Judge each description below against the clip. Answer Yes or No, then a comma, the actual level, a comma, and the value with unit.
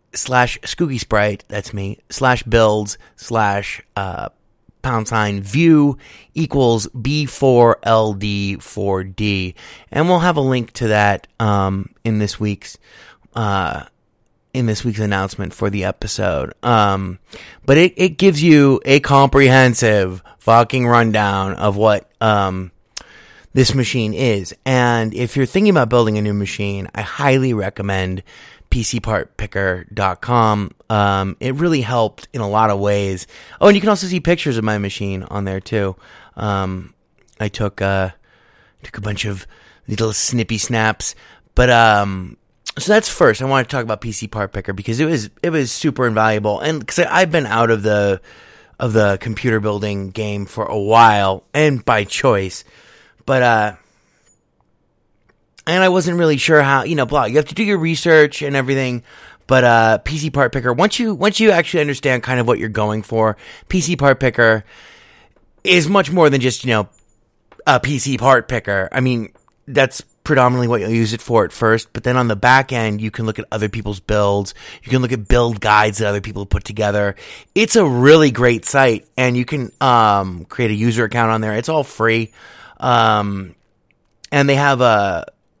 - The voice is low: Yes, low, 115 Hz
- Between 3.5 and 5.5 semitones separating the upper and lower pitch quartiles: Yes, average, 4.6 semitones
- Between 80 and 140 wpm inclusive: No, average, 170 wpm